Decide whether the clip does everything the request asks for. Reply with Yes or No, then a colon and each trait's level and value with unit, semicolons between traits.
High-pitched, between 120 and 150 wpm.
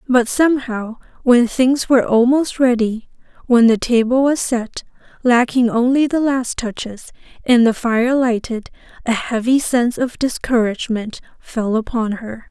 Yes: high, 240 Hz; average, 140 wpm